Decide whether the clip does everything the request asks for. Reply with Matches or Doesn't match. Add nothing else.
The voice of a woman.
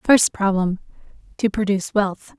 Matches